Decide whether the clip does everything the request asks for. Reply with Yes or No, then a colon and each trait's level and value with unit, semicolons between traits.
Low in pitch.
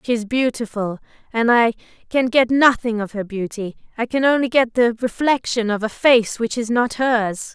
No: high, 235 Hz